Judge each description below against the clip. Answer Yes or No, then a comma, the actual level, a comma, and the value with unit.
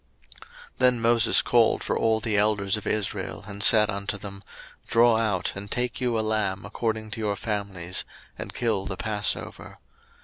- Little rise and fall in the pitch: Yes, narrow, 2.1 semitones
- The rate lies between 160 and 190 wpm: Yes, average, 170 wpm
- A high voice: No, low, 105 Hz